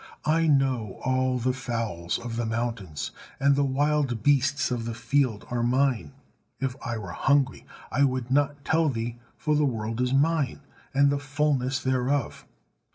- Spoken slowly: No, average, 160 wpm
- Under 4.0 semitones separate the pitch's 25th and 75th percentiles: Yes, average, 3.2 semitones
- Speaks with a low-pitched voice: Yes, low, 130 Hz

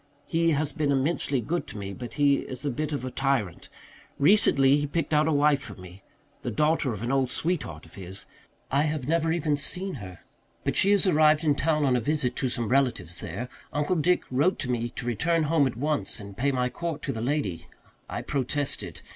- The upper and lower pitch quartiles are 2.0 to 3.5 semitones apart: No, average, 4.3 semitones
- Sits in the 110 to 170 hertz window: Yes, medium, 140 Hz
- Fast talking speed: Yes, fast, 215 wpm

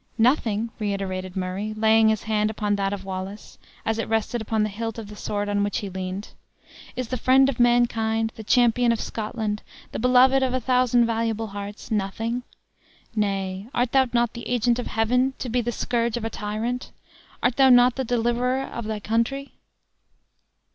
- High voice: Yes, high, 225 Hz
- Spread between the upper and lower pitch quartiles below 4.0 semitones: Yes, average, 2.8 semitones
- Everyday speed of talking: Yes, average, 180 wpm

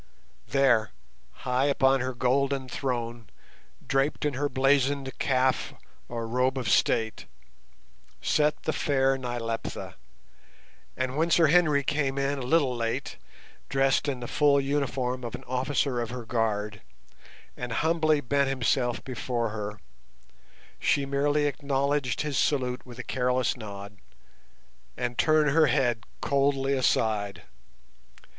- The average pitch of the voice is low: Yes, low, 130 Hz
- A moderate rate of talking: No, slow, 125 wpm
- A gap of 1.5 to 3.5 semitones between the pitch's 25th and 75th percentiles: Yes, average, 2.7 semitones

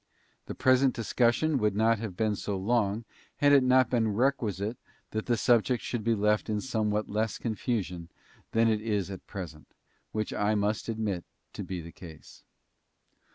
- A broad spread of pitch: No, average, 2.7 semitones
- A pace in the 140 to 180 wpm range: Yes, average, 165 wpm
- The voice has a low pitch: Yes, low, 110 Hz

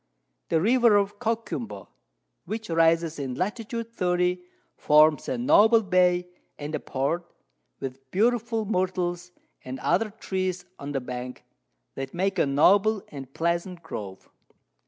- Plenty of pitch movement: Yes, wide, 5.9 semitones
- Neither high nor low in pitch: Yes, medium, 180 Hz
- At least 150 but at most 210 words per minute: No, slow, 135 wpm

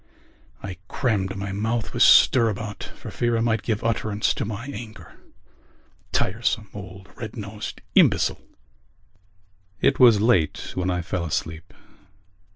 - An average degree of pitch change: Yes, average, 3.1 semitones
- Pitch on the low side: Yes, low, 105 Hz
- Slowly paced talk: Yes, slow, 130 wpm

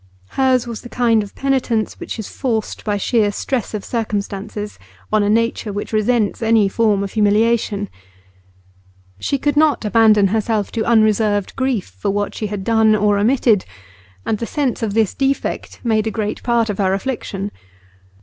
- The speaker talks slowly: No, average, 170 wpm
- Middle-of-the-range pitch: No, high, 220 Hz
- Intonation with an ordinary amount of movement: No, narrow, 2.3 semitones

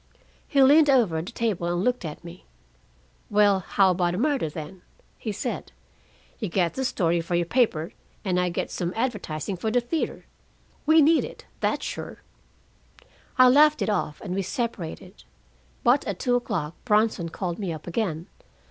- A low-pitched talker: No, high, 195 Hz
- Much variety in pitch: Yes, wide, 6.1 semitones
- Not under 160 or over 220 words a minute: Yes, average, 170 wpm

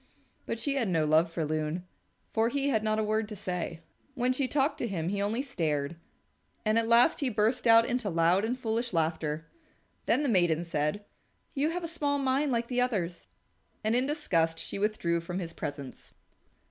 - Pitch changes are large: Yes, wide, 6.8 semitones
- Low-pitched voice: No, high, 215 Hz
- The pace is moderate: Yes, average, 195 wpm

